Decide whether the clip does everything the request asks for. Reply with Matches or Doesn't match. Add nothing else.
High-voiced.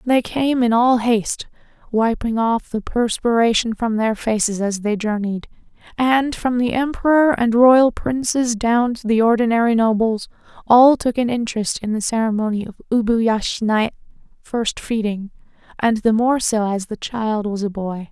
Matches